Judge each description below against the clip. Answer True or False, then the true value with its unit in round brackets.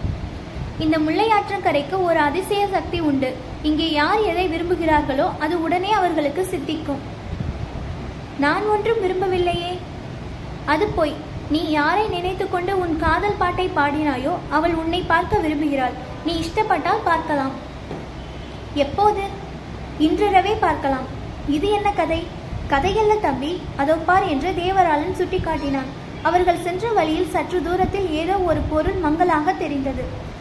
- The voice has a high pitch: True (345 Hz)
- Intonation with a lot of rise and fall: False (3.6 semitones)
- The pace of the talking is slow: False (110 wpm)